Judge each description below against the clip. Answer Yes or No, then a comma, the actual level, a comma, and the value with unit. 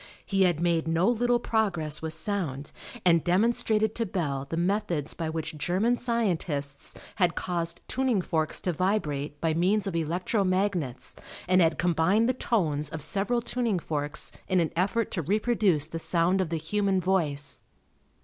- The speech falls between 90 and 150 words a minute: No, average, 160 wpm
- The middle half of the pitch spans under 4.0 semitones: No, average, 4.4 semitones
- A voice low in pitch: No, medium, 175 Hz